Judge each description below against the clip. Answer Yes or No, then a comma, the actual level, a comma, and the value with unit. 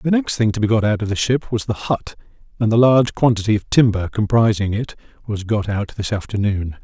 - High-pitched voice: No, low, 110 Hz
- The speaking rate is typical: No, fast, 230 wpm